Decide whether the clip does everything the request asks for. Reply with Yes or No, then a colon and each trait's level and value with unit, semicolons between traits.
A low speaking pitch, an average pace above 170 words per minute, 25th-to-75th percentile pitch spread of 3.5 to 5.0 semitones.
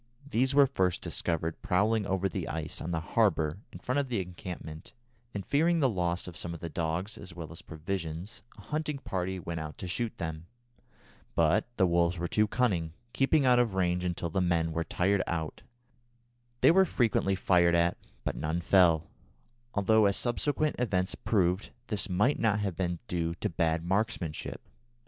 Yes: very low, 90 Hz; average, 180 wpm; average, 4.5 semitones